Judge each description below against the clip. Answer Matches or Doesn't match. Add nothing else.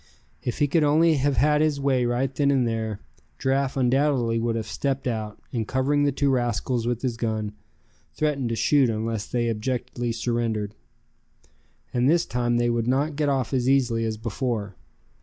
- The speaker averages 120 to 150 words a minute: Doesn't match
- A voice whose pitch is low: Matches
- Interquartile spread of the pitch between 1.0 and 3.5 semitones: Matches